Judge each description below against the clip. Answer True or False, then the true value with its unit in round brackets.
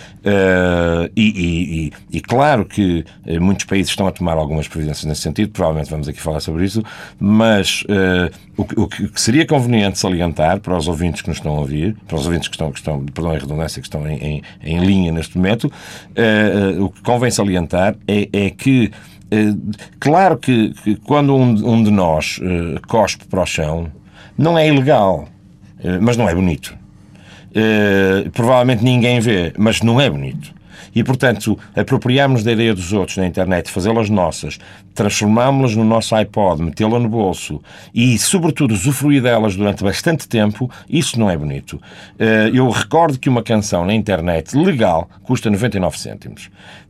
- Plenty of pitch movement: False (4.7 semitones)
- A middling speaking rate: True (175 wpm)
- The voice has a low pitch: True (100 Hz)